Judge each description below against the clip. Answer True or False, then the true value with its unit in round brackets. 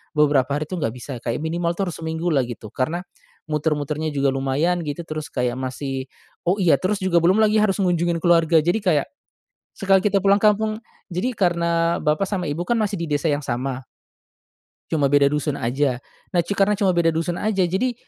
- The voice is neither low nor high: True (165 Hz)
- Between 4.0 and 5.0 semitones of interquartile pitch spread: True (4.5 semitones)